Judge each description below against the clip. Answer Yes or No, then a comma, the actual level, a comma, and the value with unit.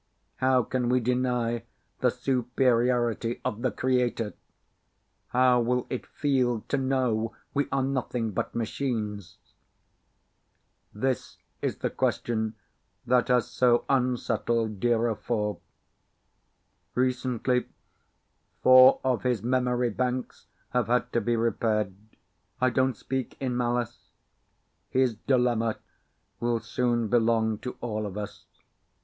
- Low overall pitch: Yes, low, 120 Hz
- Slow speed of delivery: Yes, slow, 115 wpm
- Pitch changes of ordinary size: No, narrow, 1.8 semitones